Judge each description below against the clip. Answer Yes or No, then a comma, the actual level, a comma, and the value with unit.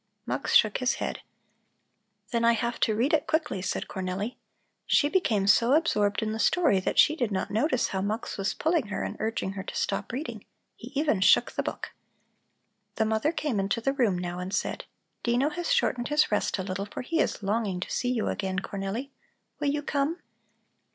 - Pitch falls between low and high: No, high, 225 Hz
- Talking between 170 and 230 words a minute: Yes, average, 200 wpm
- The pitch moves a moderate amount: No, wide, 6.2 semitones